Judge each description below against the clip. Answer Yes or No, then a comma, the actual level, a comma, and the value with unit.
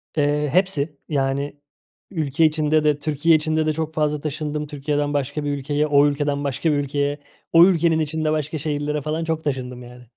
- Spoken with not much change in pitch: Yes, narrow, 1.6 semitones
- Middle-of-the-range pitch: Yes, medium, 150 Hz